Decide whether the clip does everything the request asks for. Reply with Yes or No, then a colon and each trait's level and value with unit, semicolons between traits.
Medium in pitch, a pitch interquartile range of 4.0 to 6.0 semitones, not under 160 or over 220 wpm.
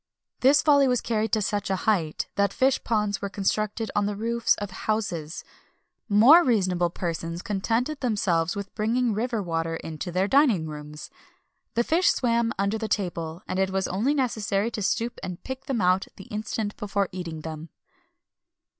No: high, 205 Hz; average, 4.3 semitones; average, 175 wpm